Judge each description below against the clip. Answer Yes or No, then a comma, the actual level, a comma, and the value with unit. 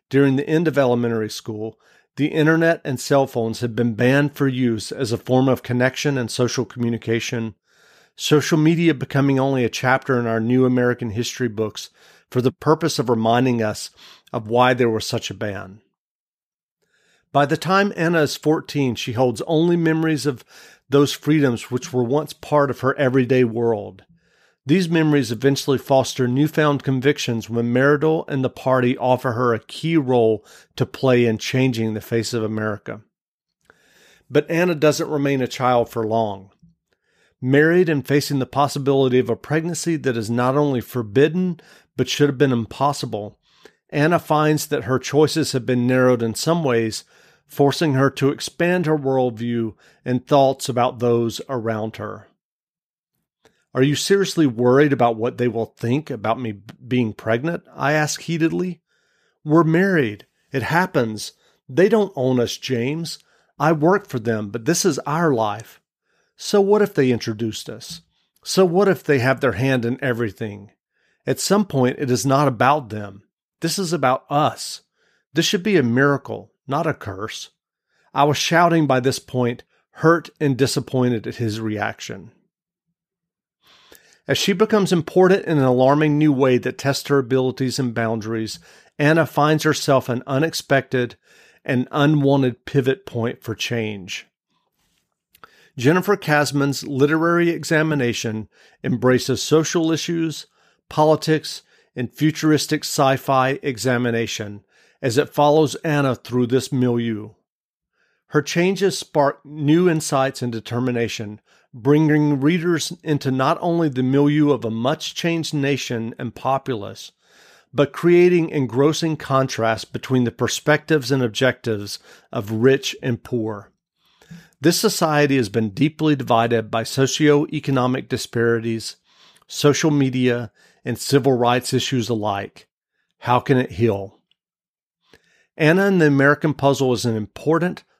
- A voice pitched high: No, low, 135 Hz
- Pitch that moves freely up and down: No, average, 4.2 semitones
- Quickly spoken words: No, average, 145 wpm